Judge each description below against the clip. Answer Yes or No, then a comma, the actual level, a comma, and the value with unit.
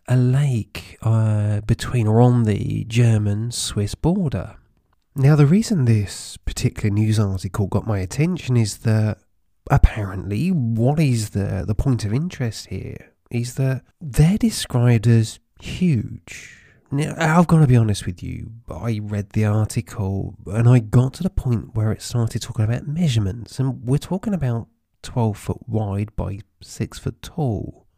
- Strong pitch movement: No, average, 4.0 semitones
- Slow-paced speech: No, average, 155 wpm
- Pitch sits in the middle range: No, low, 115 Hz